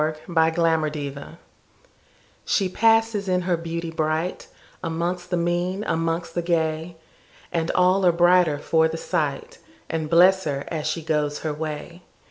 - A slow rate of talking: Yes, slow, 130 wpm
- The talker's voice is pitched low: No, medium, 165 Hz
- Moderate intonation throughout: No, narrow, 2.1 semitones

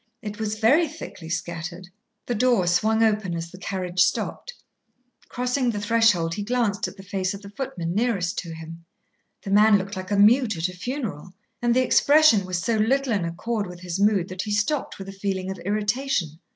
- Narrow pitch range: No, average, 4.1 semitones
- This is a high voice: Yes, high, 205 Hz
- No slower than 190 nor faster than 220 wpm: Yes, average, 200 wpm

